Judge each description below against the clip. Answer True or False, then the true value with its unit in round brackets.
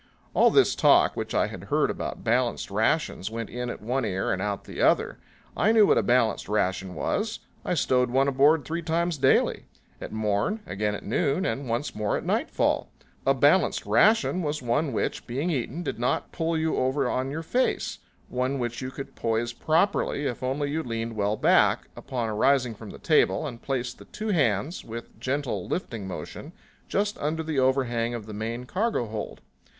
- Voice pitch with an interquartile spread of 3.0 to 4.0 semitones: False (5.3 semitones)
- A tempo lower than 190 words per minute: False (195 wpm)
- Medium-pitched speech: False (130 Hz)